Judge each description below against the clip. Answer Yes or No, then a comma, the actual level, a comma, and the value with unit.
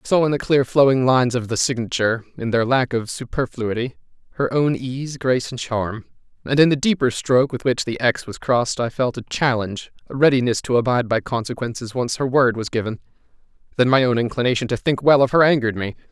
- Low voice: Yes, low, 125 Hz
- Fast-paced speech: Yes, fast, 215 wpm